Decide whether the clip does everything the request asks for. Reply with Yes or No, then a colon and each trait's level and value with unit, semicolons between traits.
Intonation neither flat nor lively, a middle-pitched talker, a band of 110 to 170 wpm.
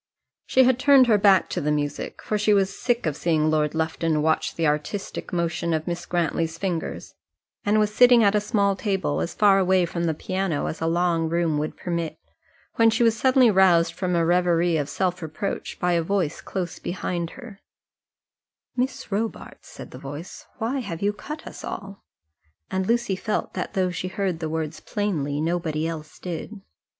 No: average, 4.1 semitones; medium, 180 Hz; average, 185 wpm